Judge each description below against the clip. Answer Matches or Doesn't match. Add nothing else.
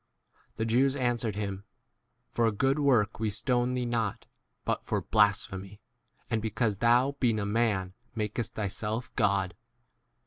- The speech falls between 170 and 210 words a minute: Doesn't match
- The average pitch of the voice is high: Doesn't match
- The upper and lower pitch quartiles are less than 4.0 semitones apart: Matches